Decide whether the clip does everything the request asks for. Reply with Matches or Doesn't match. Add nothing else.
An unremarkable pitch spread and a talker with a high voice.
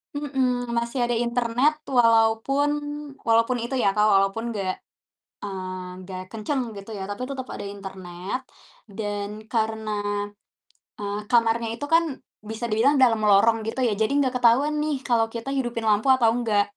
Matches